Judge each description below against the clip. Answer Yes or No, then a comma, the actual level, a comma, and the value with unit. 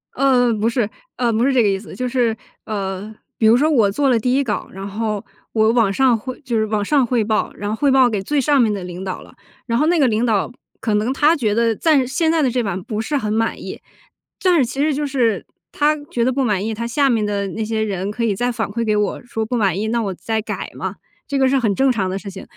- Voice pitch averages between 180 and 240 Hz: Yes, high, 230 Hz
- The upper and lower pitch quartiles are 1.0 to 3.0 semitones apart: No, average, 3.8 semitones